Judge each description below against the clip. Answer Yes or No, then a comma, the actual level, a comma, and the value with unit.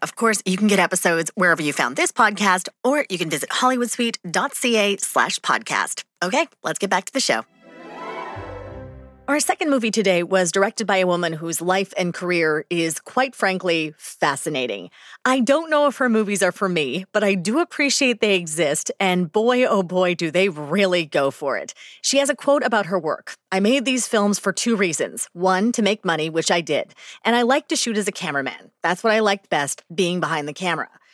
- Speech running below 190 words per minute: No, average, 200 wpm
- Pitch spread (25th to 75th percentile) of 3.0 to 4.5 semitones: No, average, 5.1 semitones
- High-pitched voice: Yes, high, 195 Hz